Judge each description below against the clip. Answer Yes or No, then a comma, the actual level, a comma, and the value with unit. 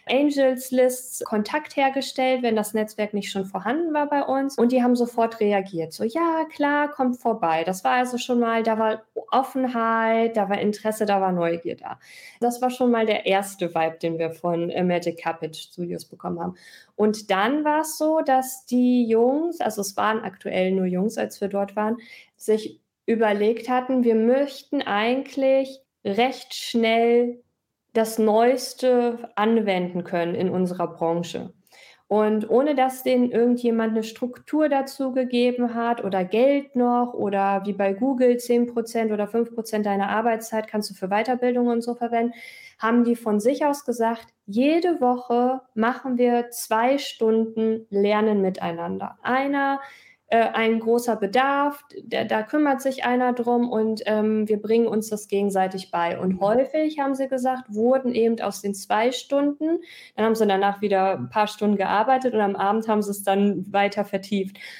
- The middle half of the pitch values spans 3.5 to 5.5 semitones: Yes, average, 3.8 semitones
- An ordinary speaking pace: Yes, average, 165 wpm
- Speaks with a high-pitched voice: Yes, high, 230 Hz